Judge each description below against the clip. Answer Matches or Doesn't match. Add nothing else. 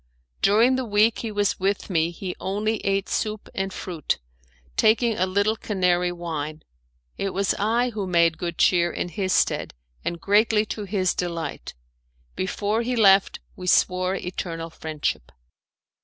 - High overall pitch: Matches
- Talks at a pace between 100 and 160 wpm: Matches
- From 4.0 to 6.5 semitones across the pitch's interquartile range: Doesn't match